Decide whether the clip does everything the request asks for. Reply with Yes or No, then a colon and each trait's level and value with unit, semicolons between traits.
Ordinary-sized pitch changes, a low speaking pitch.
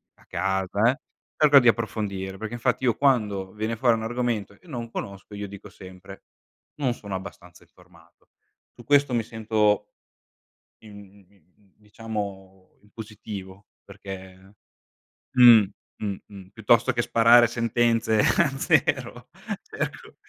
Yes: average, 3.2 semitones; low, 105 Hz